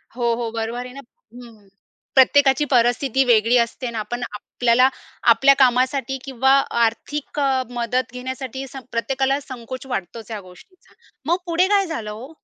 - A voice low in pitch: No, very high, 250 Hz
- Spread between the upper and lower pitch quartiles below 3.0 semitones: Yes, narrow, 2.6 semitones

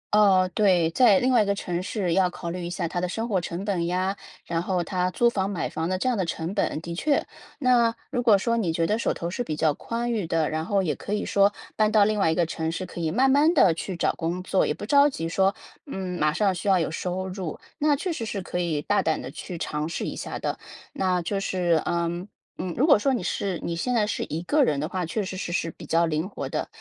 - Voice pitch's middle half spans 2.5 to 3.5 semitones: No, average, 3.9 semitones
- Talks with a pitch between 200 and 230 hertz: No, medium, 185 Hz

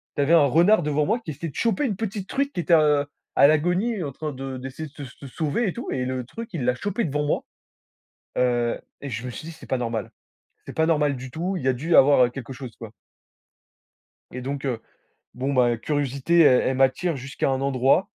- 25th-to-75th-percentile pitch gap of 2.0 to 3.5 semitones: No, average, 4.7 semitones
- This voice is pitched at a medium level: Yes, medium, 145 Hz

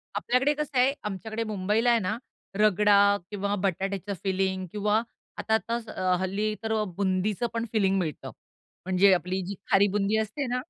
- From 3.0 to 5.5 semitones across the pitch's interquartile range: No, narrow, 2.5 semitones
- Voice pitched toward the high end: Yes, high, 205 Hz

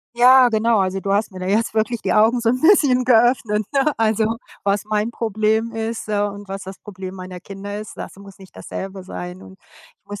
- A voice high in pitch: Yes, high, 215 Hz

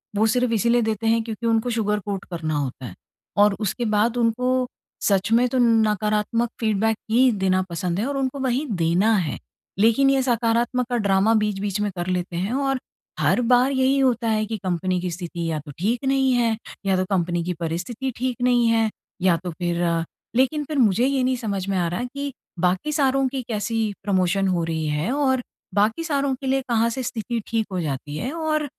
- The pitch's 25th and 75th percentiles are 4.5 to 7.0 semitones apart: Yes, average, 5.1 semitones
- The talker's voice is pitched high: Yes, high, 225 Hz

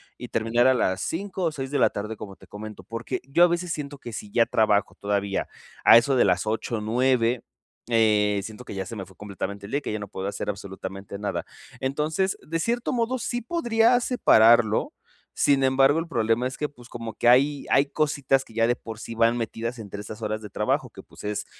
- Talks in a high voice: No, low, 115 Hz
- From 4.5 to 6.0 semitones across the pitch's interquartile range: Yes, average, 5.1 semitones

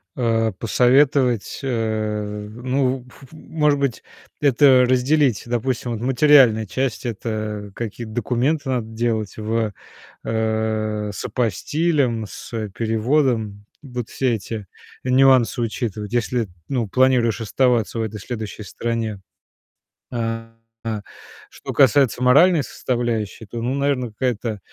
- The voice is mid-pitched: No, low, 120 Hz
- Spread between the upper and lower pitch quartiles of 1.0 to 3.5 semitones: Yes, average, 3.0 semitones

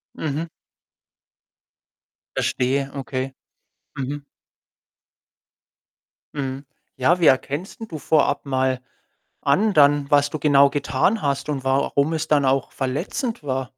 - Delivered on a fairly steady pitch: Yes, narrow, 2.2 semitones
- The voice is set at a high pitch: No, medium, 140 Hz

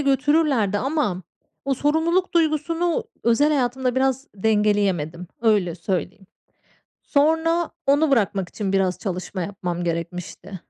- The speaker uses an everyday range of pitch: No, wide, 7.7 semitones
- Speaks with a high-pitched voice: Yes, high, 230 Hz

